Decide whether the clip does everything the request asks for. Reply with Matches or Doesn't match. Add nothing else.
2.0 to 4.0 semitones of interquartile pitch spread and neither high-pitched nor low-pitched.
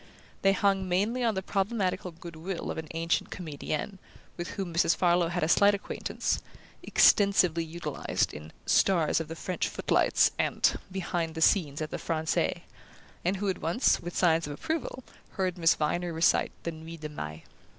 Matches